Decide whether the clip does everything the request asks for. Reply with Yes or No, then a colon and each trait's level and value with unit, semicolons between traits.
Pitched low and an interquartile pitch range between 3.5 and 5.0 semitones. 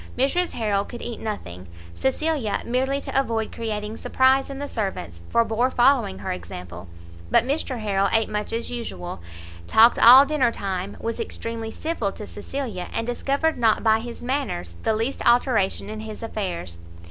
No: high, 225 Hz; average, 4.5 semitones